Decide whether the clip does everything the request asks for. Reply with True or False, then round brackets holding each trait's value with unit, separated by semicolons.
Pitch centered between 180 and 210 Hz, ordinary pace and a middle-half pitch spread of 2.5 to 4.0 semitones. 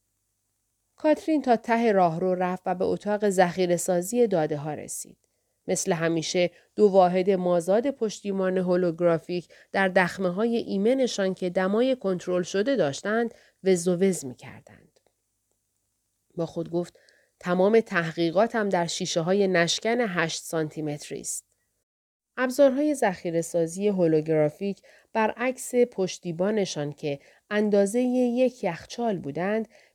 False (185 Hz; 115 wpm; 4.5 semitones)